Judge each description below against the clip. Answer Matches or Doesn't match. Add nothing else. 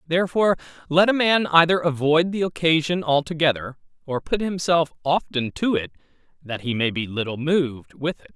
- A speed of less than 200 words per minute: Matches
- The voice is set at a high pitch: Doesn't match